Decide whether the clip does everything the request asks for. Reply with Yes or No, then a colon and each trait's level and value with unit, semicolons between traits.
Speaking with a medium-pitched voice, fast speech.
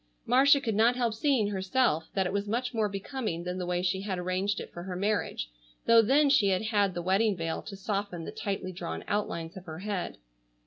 No: high, 200 Hz; fast, 220 wpm